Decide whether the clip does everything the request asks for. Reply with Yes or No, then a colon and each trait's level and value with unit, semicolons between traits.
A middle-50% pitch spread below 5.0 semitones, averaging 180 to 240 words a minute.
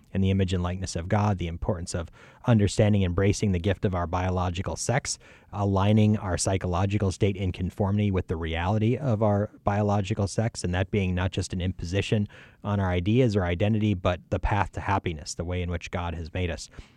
Yes: narrow, 2.6 semitones; average, 200 wpm